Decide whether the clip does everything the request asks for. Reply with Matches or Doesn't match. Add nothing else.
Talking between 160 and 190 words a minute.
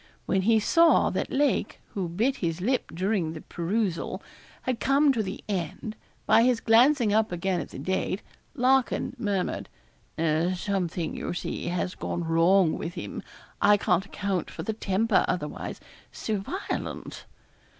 Doesn't match